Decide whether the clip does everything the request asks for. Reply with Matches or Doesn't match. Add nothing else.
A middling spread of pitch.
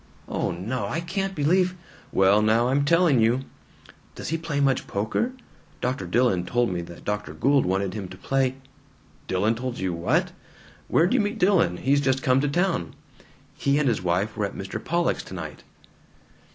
Doesn't match